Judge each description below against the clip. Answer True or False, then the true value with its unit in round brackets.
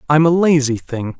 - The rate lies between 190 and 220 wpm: True (200 wpm)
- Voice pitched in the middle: True (145 Hz)